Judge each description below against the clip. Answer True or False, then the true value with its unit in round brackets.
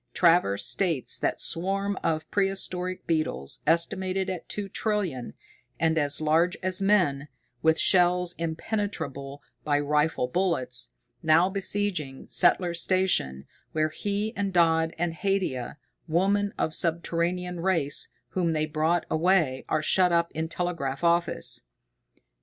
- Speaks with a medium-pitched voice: True (170 Hz)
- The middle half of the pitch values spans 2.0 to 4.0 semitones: True (3.3 semitones)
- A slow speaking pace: True (125 wpm)